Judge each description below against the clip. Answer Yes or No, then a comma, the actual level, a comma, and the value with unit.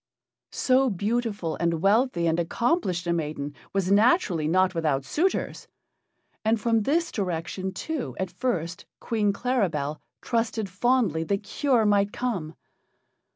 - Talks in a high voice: Yes, high, 200 Hz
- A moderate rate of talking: No, slow, 125 wpm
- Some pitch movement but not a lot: No, wide, 5.9 semitones